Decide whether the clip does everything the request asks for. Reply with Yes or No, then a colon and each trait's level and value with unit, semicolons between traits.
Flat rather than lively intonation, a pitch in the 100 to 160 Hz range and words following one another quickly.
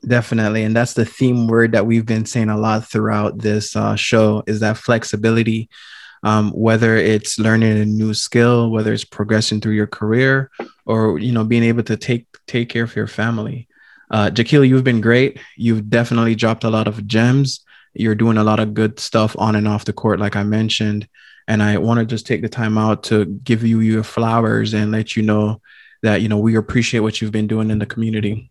Yes: narrow, 1.3 semitones; low, 110 Hz; fast, 215 wpm